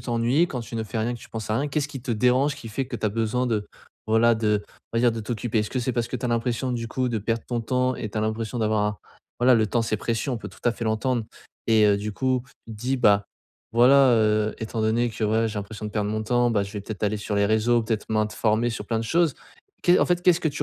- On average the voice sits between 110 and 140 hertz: Yes, low, 115 Hz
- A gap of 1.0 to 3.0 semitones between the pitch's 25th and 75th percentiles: Yes, narrow, 2.4 semitones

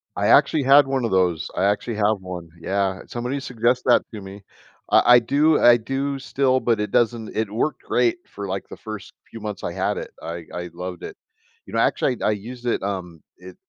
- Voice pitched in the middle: No, low, 110 Hz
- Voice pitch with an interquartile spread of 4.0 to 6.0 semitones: Yes, average, 4.5 semitones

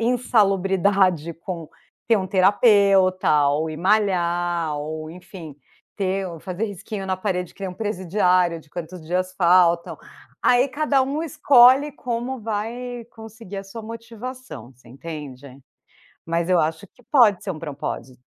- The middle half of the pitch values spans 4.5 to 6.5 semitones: Yes, average, 4.8 semitones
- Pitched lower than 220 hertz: Yes, high, 190 Hz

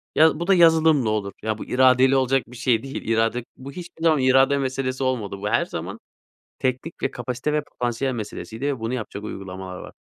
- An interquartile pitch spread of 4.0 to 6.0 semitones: No, average, 3.6 semitones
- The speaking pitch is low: Yes, low, 130 Hz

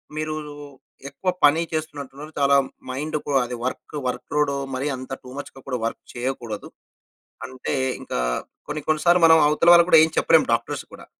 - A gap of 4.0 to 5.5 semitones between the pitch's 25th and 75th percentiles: No, average, 3.2 semitones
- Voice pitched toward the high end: No, medium, 145 Hz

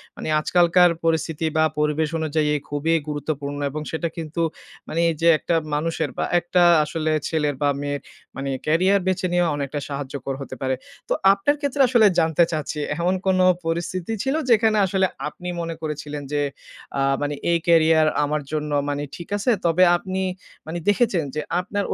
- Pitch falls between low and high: Yes, medium, 160 Hz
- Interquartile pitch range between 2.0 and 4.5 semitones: Yes, average, 3.2 semitones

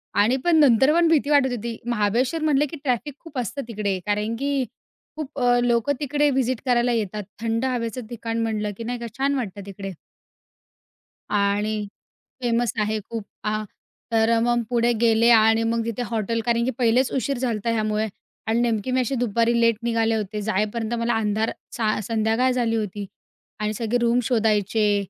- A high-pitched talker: Yes, high, 230 Hz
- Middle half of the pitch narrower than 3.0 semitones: Yes, narrow, 2.5 semitones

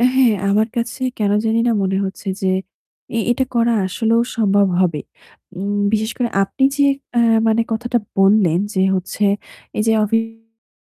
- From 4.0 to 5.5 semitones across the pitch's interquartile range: No, narrow, 2.6 semitones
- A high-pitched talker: Yes, high, 220 Hz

